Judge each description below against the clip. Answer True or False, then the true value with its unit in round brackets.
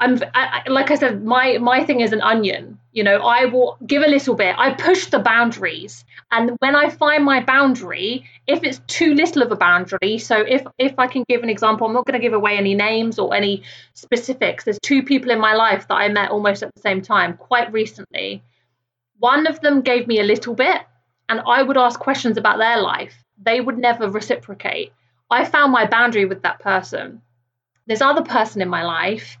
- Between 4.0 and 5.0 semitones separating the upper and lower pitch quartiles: True (4.3 semitones)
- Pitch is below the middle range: False (235 Hz)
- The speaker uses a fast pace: True (215 wpm)